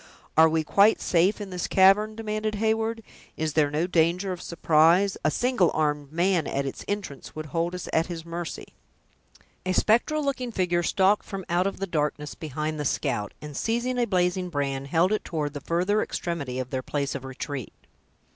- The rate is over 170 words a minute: Yes, average, 185 wpm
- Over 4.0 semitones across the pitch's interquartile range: Yes, average, 4.9 semitones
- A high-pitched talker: No, medium, 175 Hz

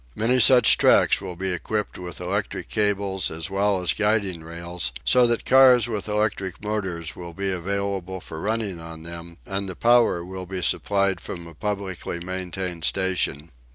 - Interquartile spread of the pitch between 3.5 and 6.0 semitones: No, average, 3.1 semitones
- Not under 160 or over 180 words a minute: Yes, average, 165 wpm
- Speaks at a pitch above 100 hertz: No, very low, 95 Hz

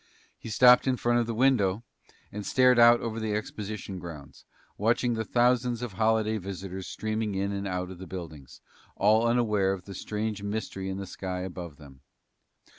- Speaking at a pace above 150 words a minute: Yes, average, 180 wpm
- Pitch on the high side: No, low, 105 Hz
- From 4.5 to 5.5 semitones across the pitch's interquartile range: No, average, 3.5 semitones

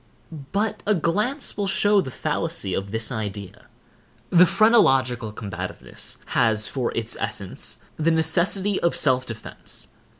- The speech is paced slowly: Yes, slow, 130 wpm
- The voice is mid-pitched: Yes, medium, 155 Hz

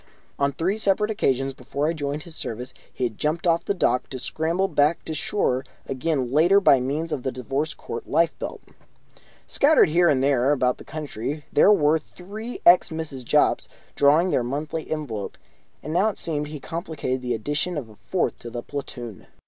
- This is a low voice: No, medium, 150 Hz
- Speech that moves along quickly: No, average, 185 wpm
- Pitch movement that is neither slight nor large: Yes, average, 4.3 semitones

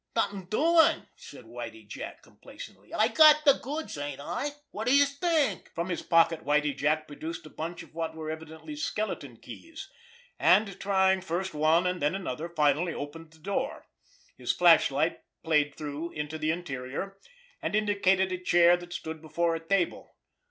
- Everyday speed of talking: Yes, average, 165 wpm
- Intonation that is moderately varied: Yes, average, 4.3 semitones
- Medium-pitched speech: Yes, medium, 170 Hz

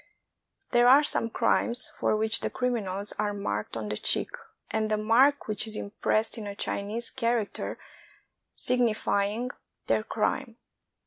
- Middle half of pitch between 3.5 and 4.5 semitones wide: No, average, 2.9 semitones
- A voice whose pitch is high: Yes, high, 220 Hz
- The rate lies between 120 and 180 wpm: Yes, average, 140 wpm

